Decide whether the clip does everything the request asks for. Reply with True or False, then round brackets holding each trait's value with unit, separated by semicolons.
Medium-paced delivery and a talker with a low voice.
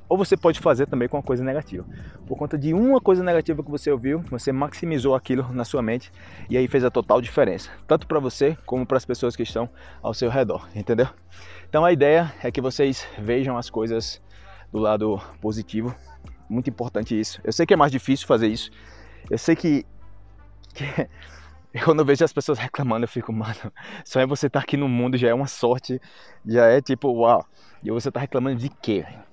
False (205 wpm; 125 Hz)